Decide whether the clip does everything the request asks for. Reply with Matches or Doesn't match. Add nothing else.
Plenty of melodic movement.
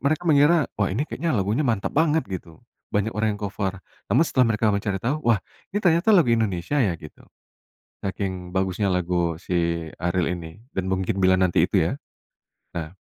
Matches